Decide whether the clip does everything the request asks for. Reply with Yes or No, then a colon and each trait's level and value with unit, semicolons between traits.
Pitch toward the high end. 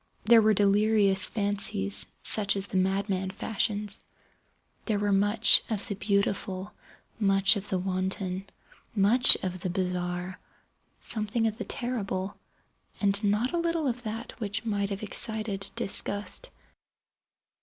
Yes: high, 200 Hz